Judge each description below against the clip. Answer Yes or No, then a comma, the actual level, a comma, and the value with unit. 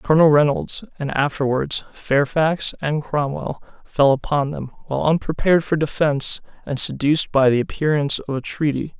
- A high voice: No, medium, 145 Hz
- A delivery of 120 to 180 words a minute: Yes, average, 145 wpm